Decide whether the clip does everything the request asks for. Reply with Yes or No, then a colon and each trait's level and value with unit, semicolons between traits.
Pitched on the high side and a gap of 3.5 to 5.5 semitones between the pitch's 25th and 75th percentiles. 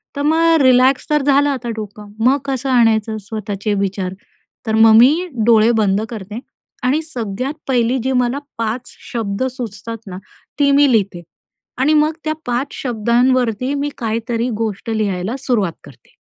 Yes: high, 235 Hz; average, 3.8 semitones